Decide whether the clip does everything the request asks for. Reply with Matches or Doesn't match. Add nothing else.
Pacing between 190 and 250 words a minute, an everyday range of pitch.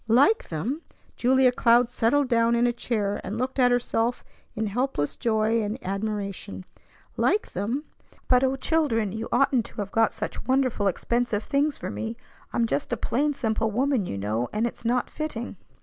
Doesn't match